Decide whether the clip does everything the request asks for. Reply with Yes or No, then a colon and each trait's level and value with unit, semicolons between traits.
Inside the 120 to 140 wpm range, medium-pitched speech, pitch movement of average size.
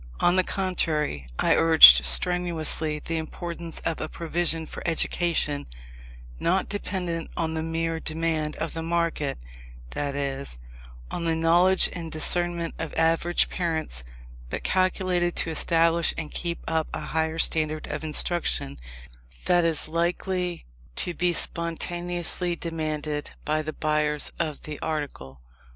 No: slow, 135 wpm; medium, 165 Hz; narrow, 2.0 semitones